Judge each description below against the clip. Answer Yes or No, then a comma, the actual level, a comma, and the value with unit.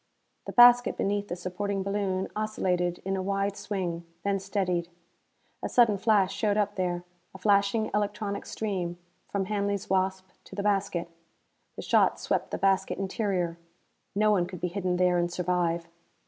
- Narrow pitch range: Yes, narrow, 2.2 semitones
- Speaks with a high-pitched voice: Yes, high, 195 Hz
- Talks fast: No, average, 160 wpm